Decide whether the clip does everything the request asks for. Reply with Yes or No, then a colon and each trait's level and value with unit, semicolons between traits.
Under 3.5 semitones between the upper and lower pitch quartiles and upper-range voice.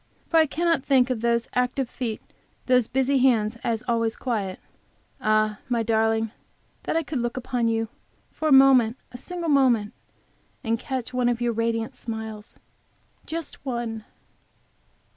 Yes: average, 2.8 semitones; high, 240 Hz